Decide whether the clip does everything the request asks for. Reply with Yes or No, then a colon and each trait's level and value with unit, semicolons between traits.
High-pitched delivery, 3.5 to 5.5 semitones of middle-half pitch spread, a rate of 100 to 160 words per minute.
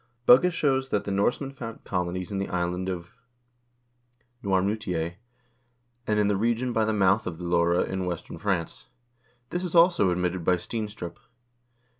No: low, 100 Hz; average, 4.2 semitones; average, 155 wpm